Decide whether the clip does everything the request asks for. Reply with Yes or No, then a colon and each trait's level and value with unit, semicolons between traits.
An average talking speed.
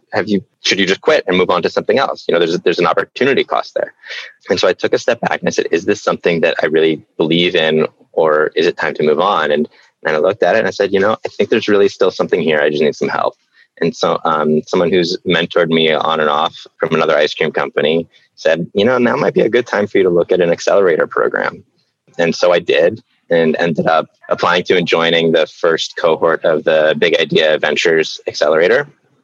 No: fast, 245 wpm